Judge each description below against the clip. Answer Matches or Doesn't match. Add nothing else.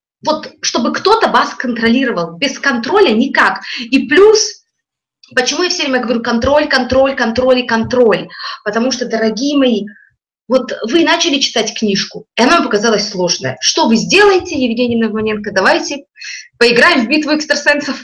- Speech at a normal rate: Matches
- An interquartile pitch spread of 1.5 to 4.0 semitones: Doesn't match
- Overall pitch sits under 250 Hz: Doesn't match